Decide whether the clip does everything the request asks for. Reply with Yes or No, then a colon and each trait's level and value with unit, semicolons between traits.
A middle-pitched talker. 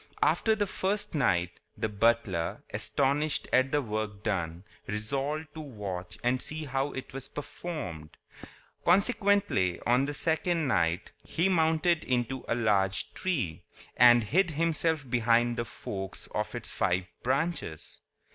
No: low, 130 Hz